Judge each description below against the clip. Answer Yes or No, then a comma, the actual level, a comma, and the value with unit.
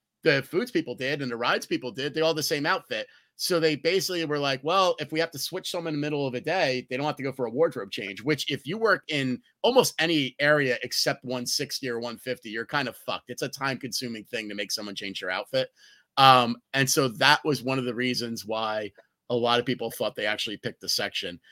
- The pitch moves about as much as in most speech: Yes, average, 3.8 semitones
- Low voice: Yes, low, 130 Hz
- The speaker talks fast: Yes, fast, 245 wpm